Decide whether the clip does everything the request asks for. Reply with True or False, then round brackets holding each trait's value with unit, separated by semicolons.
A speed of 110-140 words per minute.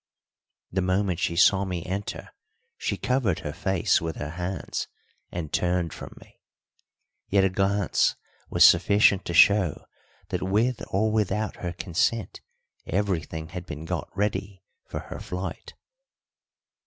True (135 wpm)